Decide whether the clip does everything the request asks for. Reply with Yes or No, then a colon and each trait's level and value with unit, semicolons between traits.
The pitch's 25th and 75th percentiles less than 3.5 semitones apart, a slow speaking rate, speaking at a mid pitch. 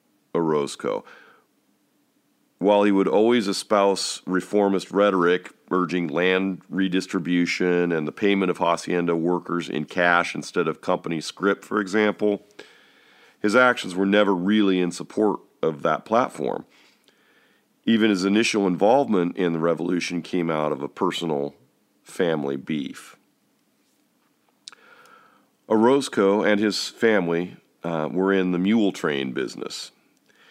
No: average, 2.7 semitones; slow, 120 wpm; very low, 95 Hz